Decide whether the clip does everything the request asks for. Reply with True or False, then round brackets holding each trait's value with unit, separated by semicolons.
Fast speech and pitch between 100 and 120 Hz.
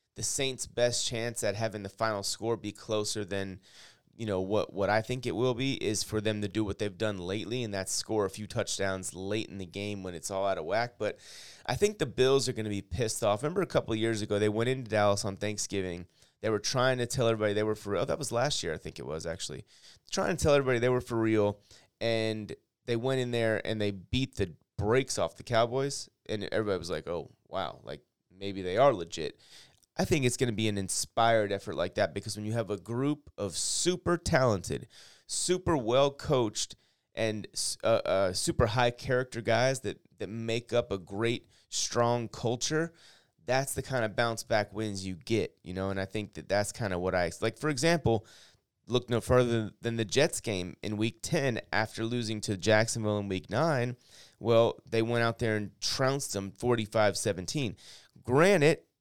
True (215 wpm; 110 Hz)